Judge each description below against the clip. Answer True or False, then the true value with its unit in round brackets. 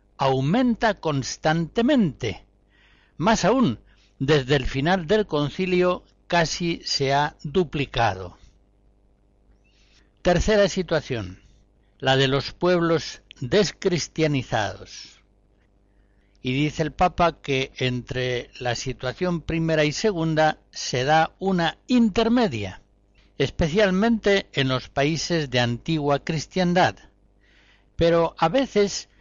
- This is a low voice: False (145 Hz)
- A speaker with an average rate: False (90 wpm)